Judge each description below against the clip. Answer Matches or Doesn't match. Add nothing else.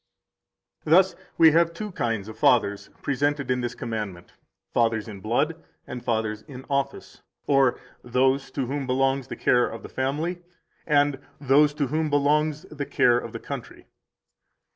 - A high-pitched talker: Doesn't match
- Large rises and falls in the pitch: Doesn't match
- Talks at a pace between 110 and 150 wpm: Doesn't match